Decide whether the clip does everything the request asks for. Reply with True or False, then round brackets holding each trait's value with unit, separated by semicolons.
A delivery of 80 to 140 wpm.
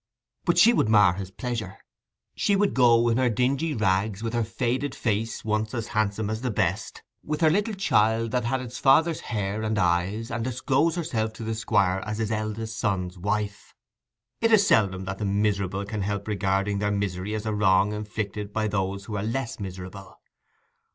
False (190 wpm)